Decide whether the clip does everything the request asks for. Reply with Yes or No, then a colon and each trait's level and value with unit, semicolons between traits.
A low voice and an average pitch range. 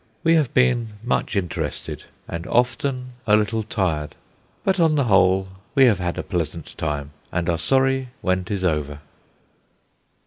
No: low, 100 Hz; wide, 6.7 semitones